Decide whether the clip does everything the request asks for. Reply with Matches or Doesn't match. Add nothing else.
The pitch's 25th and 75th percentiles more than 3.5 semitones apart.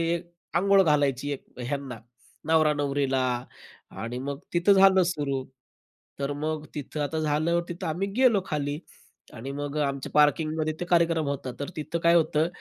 Doesn't match